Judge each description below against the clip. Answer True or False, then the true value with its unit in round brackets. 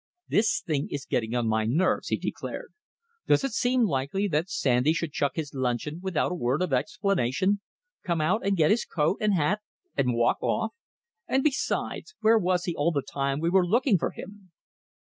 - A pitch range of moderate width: False (6.4 semitones)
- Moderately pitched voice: True (170 Hz)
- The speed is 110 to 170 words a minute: False (190 wpm)